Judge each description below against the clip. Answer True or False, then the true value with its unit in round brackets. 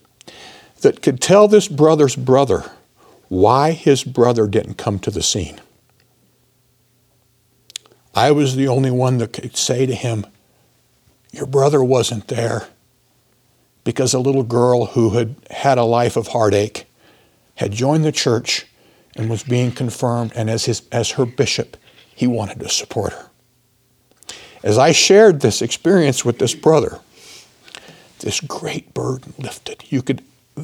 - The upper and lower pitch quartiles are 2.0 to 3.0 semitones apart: True (2.5 semitones)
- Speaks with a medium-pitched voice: False (125 Hz)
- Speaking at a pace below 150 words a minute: True (140 wpm)